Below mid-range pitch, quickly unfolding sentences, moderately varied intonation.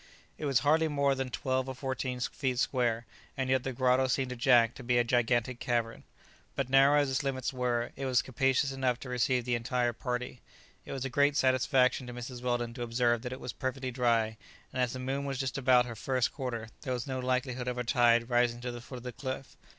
No: low, 125 Hz; fast, 230 wpm; narrow, 1.6 semitones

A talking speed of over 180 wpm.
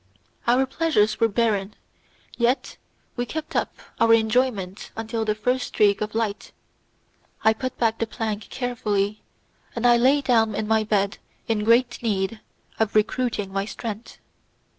No: average, 145 wpm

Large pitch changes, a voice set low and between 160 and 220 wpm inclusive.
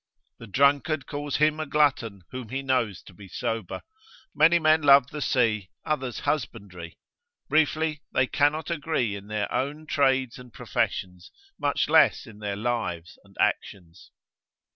No: wide, 6.0 semitones; low, 130 Hz; average, 145 wpm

